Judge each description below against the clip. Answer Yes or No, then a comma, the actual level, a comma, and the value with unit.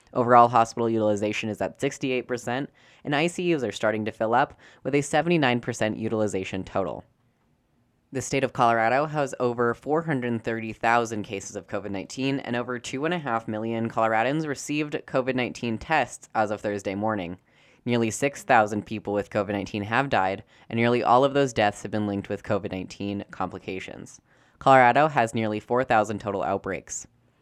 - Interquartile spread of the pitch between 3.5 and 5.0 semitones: Yes, average, 3.8 semitones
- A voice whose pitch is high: No, low, 115 Hz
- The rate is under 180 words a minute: Yes, average, 150 wpm